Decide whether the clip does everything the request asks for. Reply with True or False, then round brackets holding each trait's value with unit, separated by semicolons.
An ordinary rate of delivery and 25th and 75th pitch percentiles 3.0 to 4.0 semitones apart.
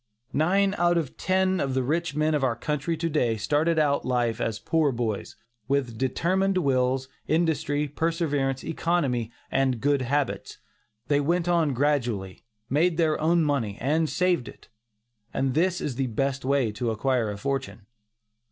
False (160 wpm; 4.4 semitones)